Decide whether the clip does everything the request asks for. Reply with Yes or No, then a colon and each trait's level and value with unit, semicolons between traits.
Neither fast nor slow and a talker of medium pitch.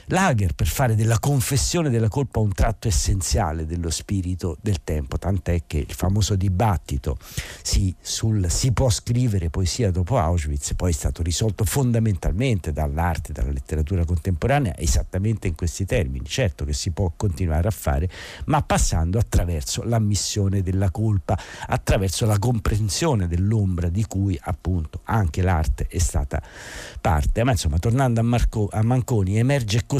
No: average, 150 wpm; very low, 95 Hz